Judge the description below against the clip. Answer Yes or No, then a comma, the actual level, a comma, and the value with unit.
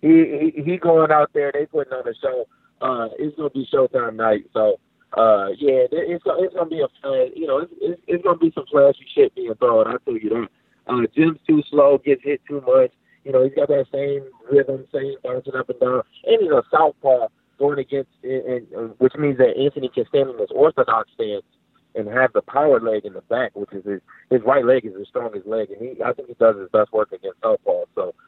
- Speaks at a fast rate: Yes, fast, 250 wpm